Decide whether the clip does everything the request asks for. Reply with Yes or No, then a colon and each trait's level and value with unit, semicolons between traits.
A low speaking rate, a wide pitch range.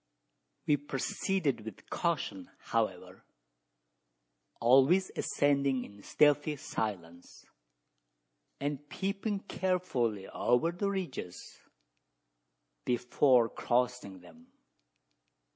Yes: slow, 75 wpm; wide, 6.7 semitones